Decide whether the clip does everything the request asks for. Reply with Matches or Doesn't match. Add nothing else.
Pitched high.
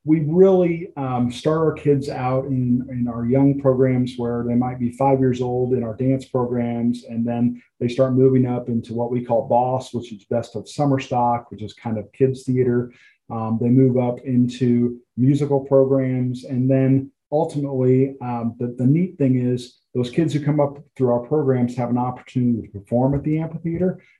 Doesn't match